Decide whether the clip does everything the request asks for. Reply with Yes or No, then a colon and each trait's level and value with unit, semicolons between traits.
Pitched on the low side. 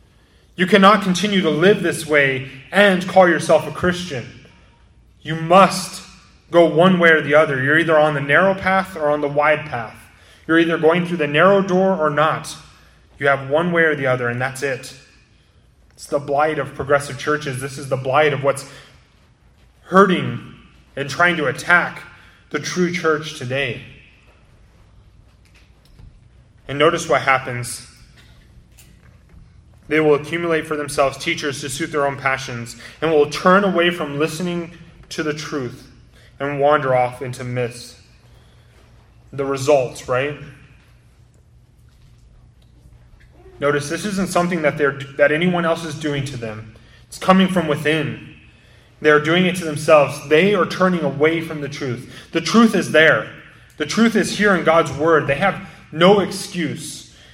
No: medium, 150 Hz